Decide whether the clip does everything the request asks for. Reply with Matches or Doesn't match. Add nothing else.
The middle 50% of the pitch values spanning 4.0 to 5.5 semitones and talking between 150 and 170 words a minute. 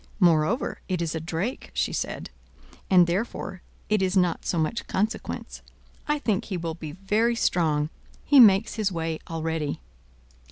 Matches